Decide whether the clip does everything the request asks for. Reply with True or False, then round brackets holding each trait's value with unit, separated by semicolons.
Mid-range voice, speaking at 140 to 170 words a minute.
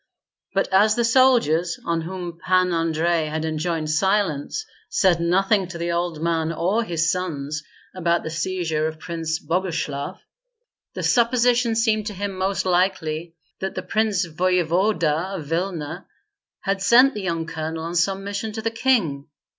True (175 Hz; 155 wpm)